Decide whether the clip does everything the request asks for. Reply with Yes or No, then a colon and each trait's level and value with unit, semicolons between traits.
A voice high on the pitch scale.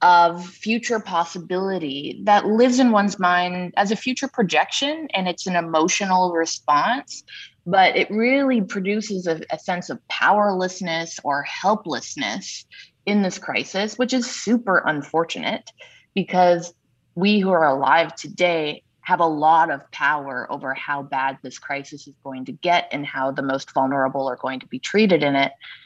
No: medium, 180 Hz